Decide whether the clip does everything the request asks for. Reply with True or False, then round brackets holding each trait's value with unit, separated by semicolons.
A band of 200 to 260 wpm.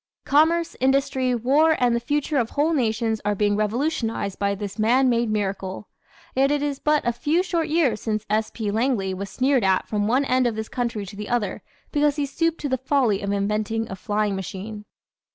True (205 wpm)